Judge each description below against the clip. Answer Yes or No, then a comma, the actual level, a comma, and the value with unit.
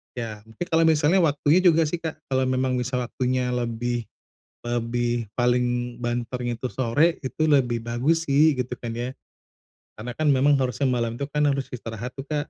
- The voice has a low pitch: Yes, low, 125 Hz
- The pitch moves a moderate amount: Yes, average, 3.4 semitones